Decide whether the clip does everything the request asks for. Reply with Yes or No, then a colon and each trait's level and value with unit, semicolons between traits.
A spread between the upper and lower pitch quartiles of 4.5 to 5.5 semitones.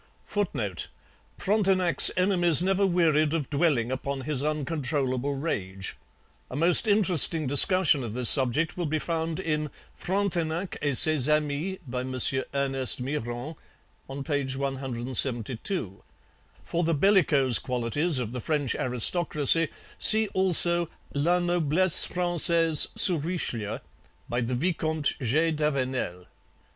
Yes: average, 4.9 semitones